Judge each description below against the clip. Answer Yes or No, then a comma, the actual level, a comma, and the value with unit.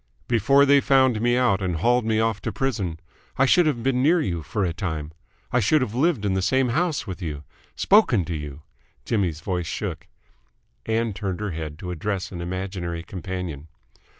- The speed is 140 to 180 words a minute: No, average, 195 wpm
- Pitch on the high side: No, low, 100 Hz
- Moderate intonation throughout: No, wide, 6.3 semitones